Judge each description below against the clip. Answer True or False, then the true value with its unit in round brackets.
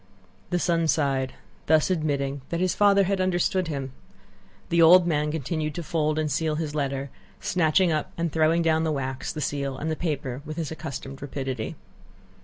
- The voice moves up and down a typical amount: True (3.1 semitones)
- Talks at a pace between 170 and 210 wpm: True (180 wpm)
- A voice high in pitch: False (155 Hz)